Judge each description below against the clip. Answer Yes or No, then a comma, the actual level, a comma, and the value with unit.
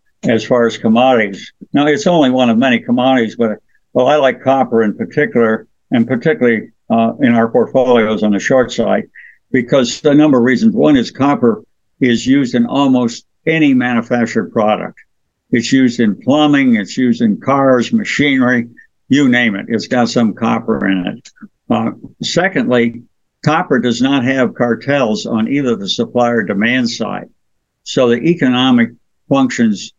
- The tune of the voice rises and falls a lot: Yes, wide, 6.4 semitones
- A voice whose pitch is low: Yes, low, 130 Hz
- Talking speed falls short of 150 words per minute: No, average, 160 wpm